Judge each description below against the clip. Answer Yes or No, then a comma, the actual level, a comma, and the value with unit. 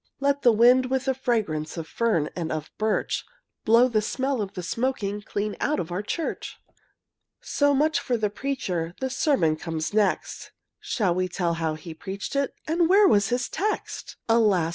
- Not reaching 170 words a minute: No, average, 180 wpm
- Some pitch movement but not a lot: No, wide, 6.9 semitones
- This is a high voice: Yes, high, 215 Hz